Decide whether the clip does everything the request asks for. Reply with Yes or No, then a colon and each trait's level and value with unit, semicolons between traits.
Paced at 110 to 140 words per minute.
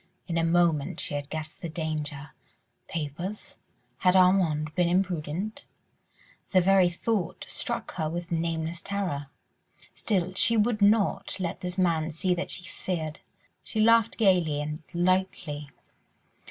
Yes: slow, 135 wpm